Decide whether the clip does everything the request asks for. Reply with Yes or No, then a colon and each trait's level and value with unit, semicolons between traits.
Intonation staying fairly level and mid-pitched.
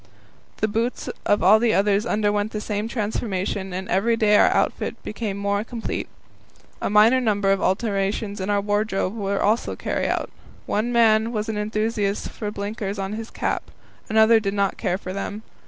No: narrow, 1.7 semitones; high, 210 Hz